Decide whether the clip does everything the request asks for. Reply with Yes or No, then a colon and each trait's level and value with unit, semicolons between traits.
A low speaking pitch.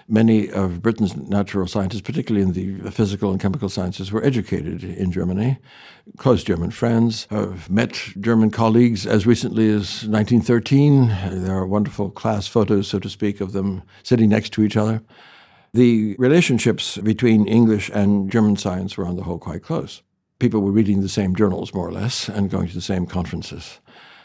Yes: low, 105 Hz